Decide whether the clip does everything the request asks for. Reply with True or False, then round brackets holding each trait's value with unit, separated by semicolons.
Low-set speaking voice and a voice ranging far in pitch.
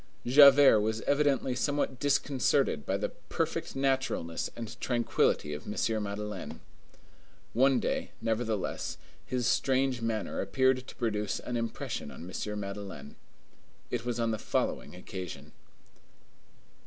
False (115 Hz; 4.1 semitones)